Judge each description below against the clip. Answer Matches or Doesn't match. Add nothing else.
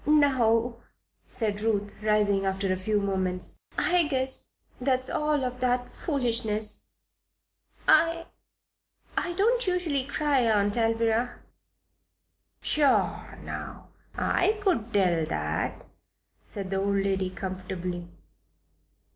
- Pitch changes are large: Matches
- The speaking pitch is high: Matches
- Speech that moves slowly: Matches